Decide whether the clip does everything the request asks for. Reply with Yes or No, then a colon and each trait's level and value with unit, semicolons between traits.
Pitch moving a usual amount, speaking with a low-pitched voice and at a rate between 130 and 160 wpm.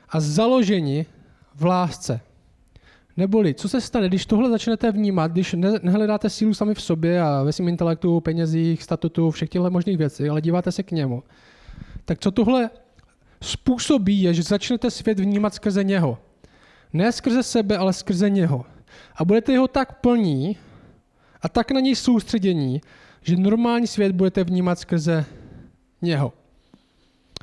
No: average, 5.0 semitones; medium, 185 Hz; average, 150 wpm